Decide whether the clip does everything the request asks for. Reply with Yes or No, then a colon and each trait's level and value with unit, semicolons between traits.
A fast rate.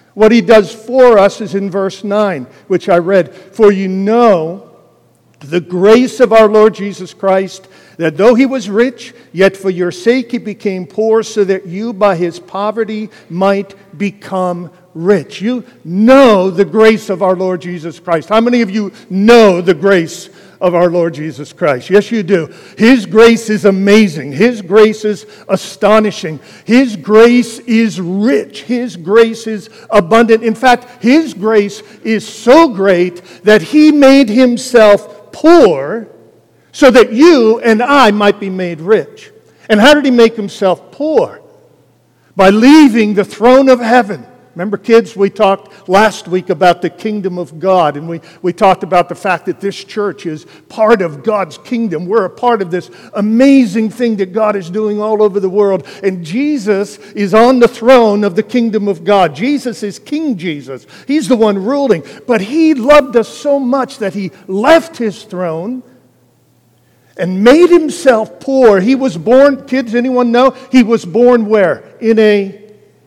No: average, 170 wpm